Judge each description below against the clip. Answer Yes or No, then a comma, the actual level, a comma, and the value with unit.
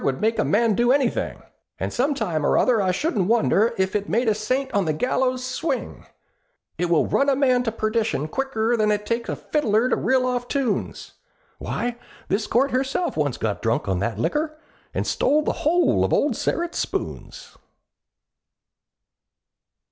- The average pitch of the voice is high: Yes, high, 235 Hz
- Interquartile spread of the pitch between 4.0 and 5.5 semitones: Yes, average, 4.5 semitones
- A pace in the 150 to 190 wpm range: Yes, average, 175 wpm